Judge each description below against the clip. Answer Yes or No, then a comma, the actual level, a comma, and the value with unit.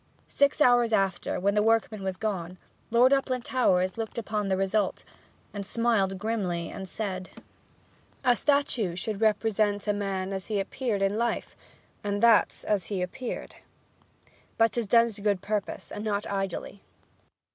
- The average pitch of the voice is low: No, high, 210 Hz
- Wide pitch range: No, average, 2.9 semitones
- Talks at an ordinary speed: Yes, average, 155 wpm